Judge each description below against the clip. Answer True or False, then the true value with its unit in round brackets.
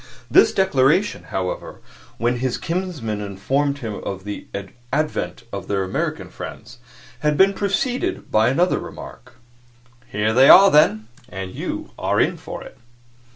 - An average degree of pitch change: False (8.5 semitones)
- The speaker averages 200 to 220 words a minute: False (140 wpm)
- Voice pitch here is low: True (130 Hz)